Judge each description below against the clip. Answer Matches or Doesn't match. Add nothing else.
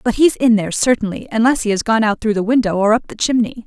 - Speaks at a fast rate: Matches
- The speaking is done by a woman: Matches